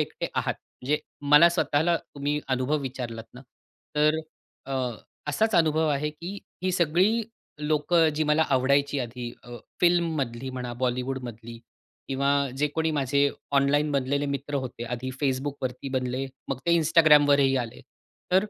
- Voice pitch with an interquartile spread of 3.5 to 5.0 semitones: No, average, 2.9 semitones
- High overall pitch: No, medium, 140 Hz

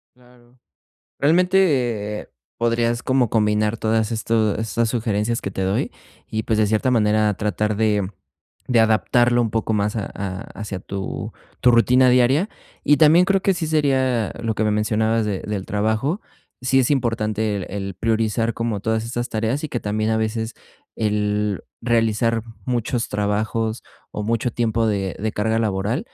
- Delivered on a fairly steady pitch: Yes, narrow, 2.3 semitones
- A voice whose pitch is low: Yes, low, 110 Hz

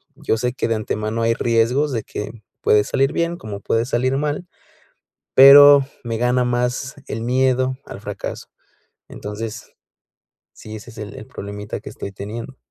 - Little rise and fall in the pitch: No, average, 3.3 semitones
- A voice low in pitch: Yes, low, 120 Hz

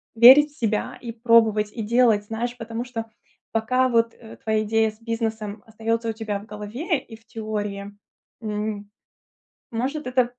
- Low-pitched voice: No, high, 225 Hz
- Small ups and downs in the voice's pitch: Yes, narrow, 1.9 semitones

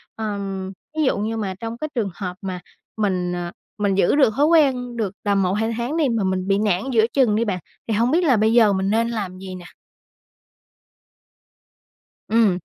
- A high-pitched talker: Yes, high, 215 Hz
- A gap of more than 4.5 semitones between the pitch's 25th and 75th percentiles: No, average, 3.6 semitones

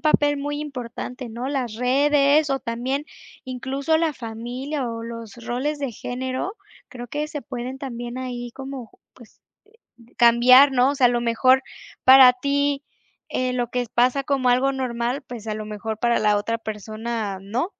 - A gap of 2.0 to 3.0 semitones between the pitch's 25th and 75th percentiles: Yes, average, 2.7 semitones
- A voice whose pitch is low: No, very high, 250 Hz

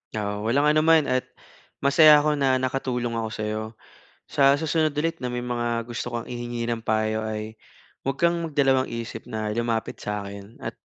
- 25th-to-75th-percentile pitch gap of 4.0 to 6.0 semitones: Yes, average, 4.3 semitones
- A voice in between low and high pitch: No, low, 120 Hz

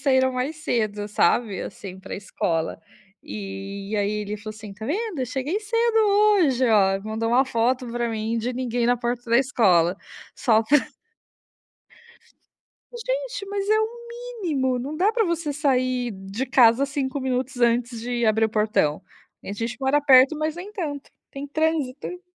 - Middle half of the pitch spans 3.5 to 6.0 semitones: Yes, average, 5.2 semitones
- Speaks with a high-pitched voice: Yes, very high, 250 Hz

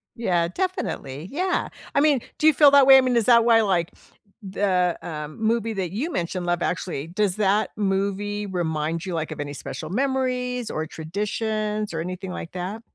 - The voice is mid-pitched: No, high, 200 Hz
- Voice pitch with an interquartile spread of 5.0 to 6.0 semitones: Yes, average, 5.3 semitones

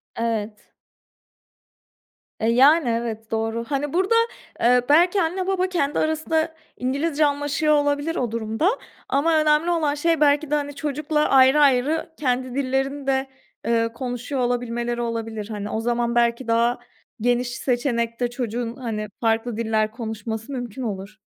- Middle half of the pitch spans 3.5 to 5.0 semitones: Yes, average, 4.2 semitones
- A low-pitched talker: No, very high, 250 Hz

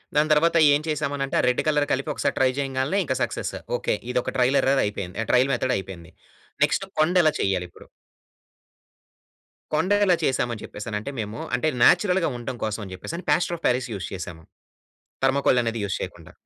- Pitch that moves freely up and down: Yes, wide, 5.7 semitones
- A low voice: Yes, low, 130 Hz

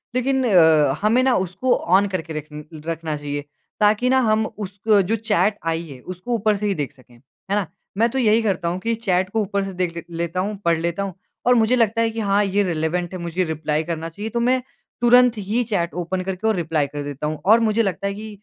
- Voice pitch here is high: Yes, high, 195 Hz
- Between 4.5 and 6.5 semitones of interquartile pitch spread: Yes, average, 4.8 semitones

